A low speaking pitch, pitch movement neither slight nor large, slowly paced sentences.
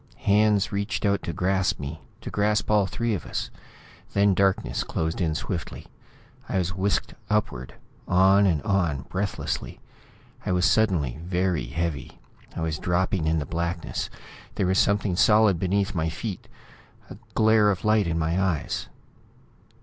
No: very low, 95 Hz; average, 3.4 semitones; average, 150 wpm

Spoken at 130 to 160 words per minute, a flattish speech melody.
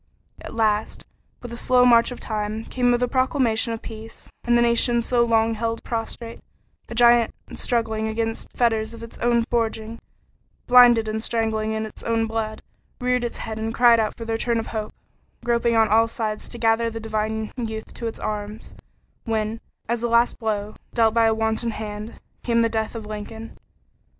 No: average, 185 wpm; narrow, 1.3 semitones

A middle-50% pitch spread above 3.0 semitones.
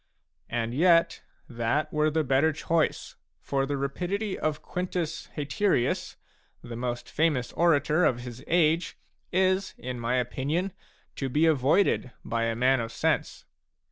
Yes: average, 5.1 semitones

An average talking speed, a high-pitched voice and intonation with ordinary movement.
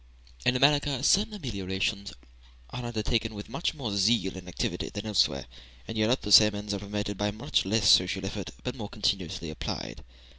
No: average, 170 wpm; low, 105 Hz; average, 3.3 semitones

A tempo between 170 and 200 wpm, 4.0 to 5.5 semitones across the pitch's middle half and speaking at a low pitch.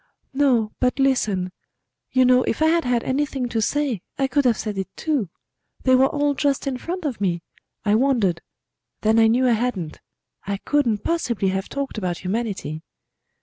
No: average, 180 wpm; average, 5.0 semitones; high, 245 Hz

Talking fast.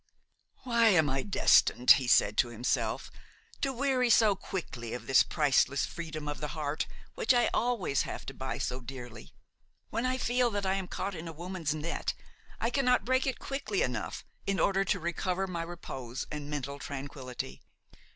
No: average, 175 wpm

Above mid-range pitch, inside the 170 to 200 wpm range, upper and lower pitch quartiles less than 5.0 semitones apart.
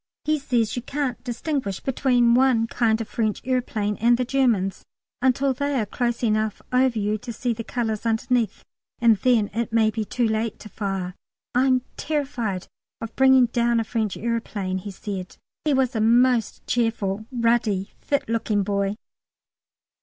No: high, 230 Hz; average, 160 wpm; average, 2.8 semitones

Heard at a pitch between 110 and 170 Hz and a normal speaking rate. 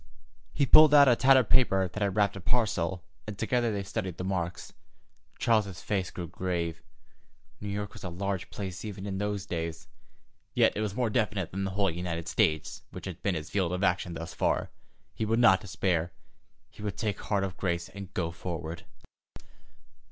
No: very low, 95 Hz; average, 190 wpm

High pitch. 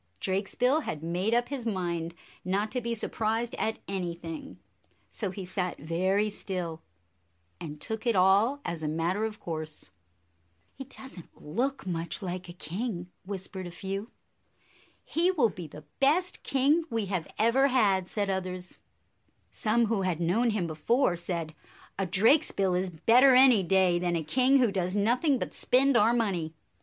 Yes: high, 195 Hz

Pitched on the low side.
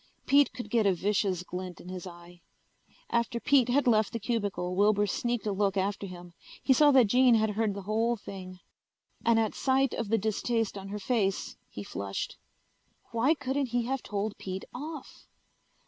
No: high, 215 Hz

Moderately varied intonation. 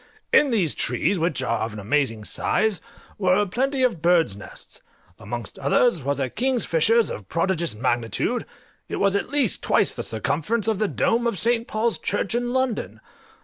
No: wide, 8.8 semitones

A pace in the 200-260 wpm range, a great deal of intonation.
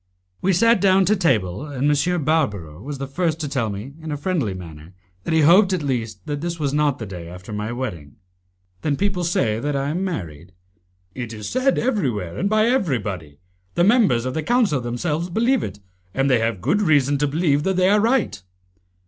Yes: fast, 205 wpm; wide, 8.4 semitones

